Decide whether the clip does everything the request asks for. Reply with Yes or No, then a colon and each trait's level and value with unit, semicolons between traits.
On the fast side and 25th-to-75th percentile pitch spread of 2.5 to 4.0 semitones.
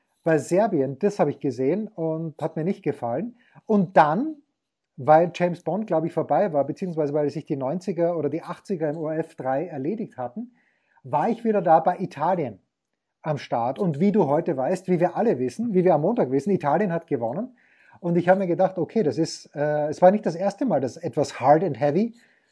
No: fast, 210 wpm; average, 4.7 semitones